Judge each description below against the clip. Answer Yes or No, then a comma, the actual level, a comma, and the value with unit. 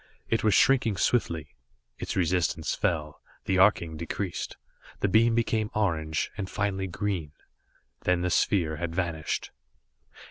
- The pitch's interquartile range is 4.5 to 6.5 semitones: No, average, 4.1 semitones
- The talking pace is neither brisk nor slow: No, slow, 130 wpm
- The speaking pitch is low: Yes, very low, 90 Hz